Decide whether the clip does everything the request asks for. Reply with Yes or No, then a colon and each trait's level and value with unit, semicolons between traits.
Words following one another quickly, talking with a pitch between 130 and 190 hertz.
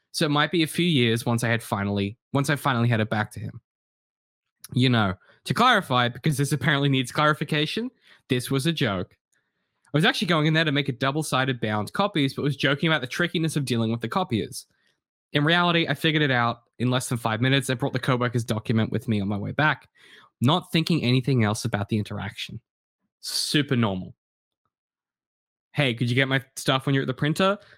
Yes: fast, 210 wpm; low, 135 Hz